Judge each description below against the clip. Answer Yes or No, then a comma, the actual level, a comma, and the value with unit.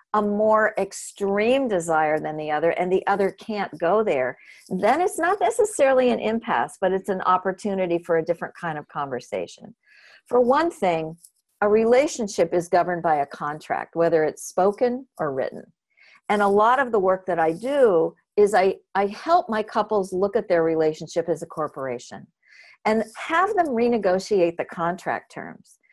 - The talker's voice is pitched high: Yes, high, 200 Hz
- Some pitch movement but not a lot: No, wide, 6.3 semitones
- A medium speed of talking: Yes, average, 170 wpm